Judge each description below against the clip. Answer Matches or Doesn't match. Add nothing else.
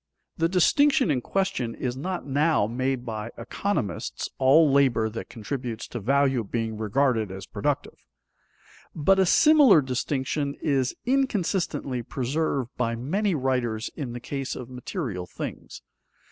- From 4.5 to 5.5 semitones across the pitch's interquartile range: Matches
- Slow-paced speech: Matches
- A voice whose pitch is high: Doesn't match